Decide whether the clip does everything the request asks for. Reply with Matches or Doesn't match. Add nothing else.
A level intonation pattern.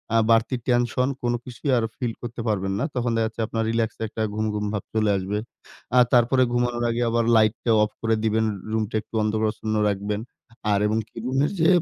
Matches